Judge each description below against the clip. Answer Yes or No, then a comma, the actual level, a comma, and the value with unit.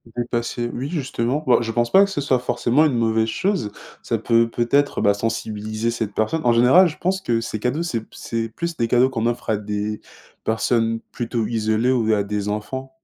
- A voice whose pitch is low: Yes, low, 120 Hz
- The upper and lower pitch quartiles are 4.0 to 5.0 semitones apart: No, average, 2.9 semitones